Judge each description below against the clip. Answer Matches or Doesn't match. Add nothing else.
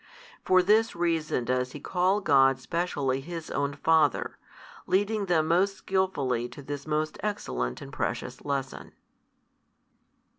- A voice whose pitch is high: Doesn't match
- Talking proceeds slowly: Matches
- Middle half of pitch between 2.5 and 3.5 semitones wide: Doesn't match